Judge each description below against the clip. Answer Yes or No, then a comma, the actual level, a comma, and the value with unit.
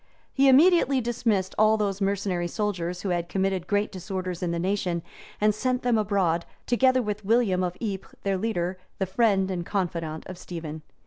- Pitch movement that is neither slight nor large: Yes, average, 3.2 semitones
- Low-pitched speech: No, high, 195 Hz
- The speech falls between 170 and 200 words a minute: Yes, average, 180 wpm